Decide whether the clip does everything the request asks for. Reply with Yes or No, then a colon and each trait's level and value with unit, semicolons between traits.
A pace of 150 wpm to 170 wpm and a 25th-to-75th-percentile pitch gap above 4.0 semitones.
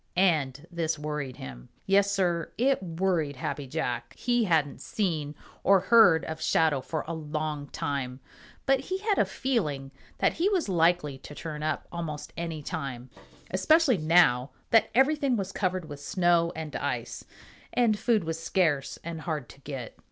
Yes: average, 160 wpm; average, 4.8 semitones